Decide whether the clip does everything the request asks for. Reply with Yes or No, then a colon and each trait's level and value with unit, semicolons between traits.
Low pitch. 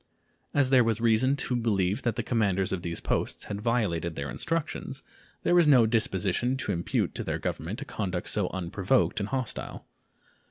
Yes: low, 110 Hz